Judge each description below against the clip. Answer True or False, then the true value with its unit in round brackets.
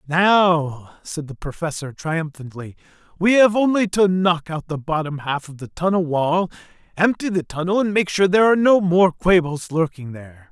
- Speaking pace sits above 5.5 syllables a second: False (4.8 syllables/s)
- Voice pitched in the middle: True (170 Hz)